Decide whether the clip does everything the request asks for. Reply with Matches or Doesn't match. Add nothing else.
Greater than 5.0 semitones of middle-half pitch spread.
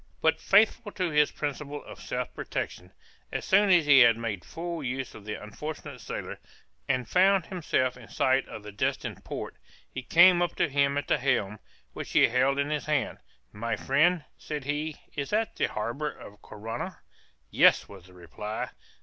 Matches